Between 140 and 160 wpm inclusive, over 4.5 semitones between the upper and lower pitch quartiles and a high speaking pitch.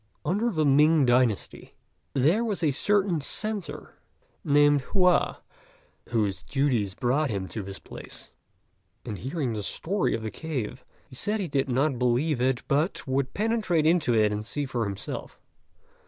No: average, 155 wpm; wide, 5.5 semitones; medium, 140 Hz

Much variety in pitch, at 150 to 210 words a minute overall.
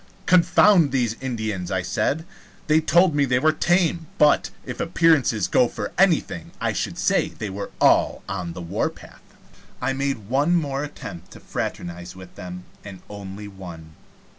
Yes: wide, 8.7 semitones; average, 160 wpm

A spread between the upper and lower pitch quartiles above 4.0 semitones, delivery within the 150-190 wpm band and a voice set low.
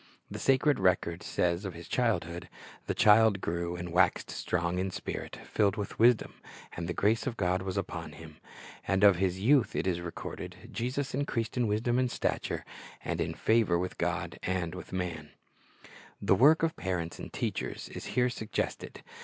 Yes: average, 5.0 semitones; average, 170 wpm; very low, 95 Hz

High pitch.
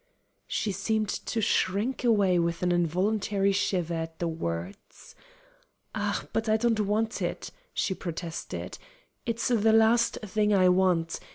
Yes: high, 195 Hz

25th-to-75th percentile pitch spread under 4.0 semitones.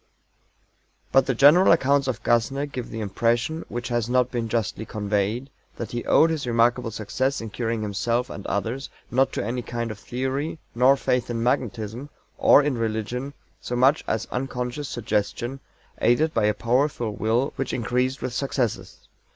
Yes: average, 2.8 semitones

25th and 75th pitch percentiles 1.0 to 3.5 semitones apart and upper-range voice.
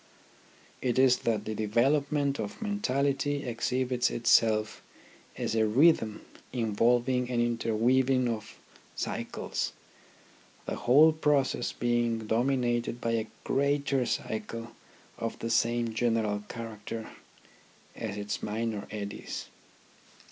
No: average, 2.8 semitones; low, 120 Hz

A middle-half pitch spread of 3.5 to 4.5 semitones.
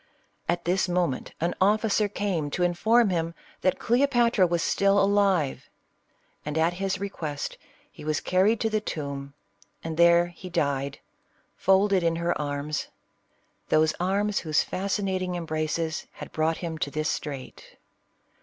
Yes: average, 4.0 semitones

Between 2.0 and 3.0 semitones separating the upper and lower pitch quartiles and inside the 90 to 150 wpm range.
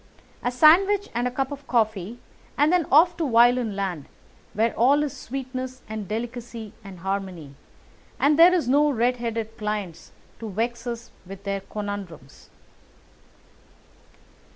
No: average, 4.8 semitones; average, 140 wpm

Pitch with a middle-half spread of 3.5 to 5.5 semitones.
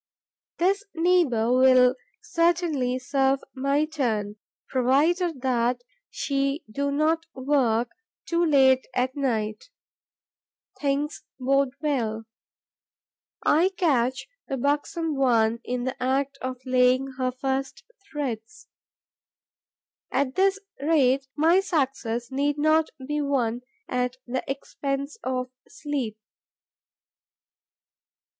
No: average, 2.9 semitones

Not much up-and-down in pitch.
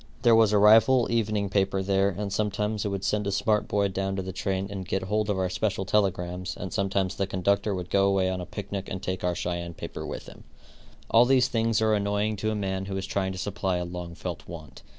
Yes: narrow, 2.0 semitones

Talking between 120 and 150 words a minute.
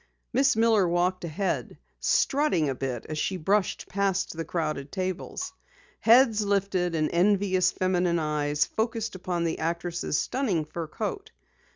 Yes: average, 140 wpm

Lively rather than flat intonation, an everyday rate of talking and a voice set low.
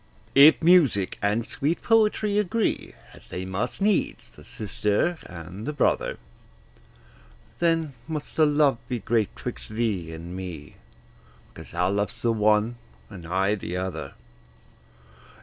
No: wide, 8.9 semitones; slow, 130 wpm; low, 110 Hz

